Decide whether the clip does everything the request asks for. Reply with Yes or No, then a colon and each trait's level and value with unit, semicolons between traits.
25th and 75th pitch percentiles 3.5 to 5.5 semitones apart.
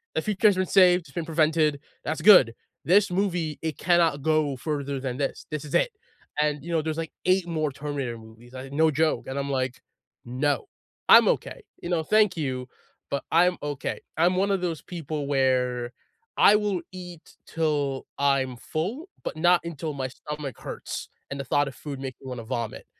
Yes: average, 4.2 semitones